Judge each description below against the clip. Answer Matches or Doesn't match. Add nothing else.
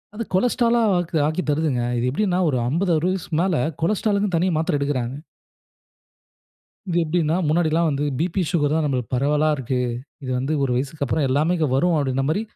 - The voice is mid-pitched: Matches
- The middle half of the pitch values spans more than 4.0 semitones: Matches